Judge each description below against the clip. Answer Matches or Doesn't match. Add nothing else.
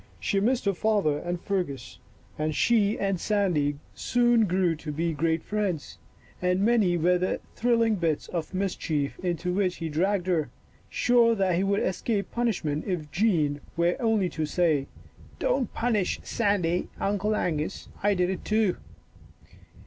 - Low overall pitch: Doesn't match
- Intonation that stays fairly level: Doesn't match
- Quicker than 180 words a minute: Doesn't match